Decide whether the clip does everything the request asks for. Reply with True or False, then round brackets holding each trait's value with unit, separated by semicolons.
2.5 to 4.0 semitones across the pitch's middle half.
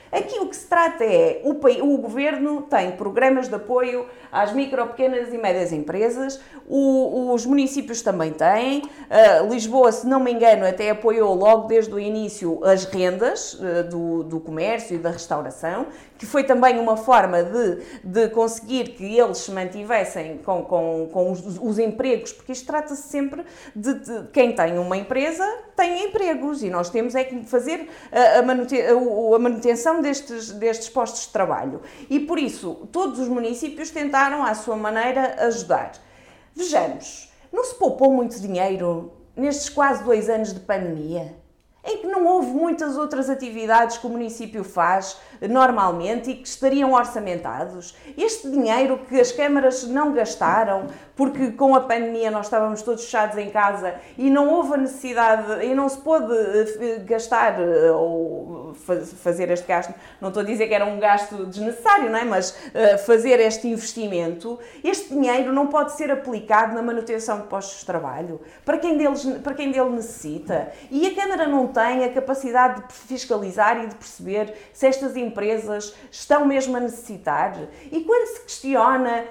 False (4.7 semitones)